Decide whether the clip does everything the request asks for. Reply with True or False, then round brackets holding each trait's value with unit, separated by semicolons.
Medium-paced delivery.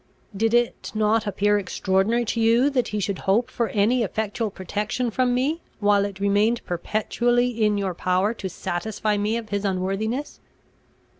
True (160 wpm)